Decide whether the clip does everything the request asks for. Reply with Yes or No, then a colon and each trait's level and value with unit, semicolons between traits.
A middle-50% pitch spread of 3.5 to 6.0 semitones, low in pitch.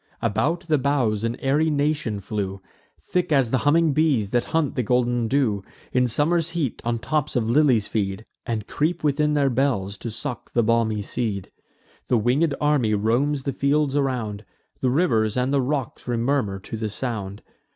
Yes: average, 4.9 semitones; low, 125 Hz